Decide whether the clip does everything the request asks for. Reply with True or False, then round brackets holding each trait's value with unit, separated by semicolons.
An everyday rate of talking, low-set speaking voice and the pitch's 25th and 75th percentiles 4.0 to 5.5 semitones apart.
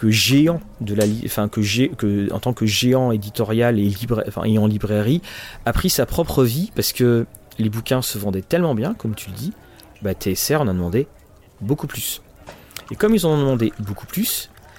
True (205 wpm; 110 Hz; 4.3 semitones)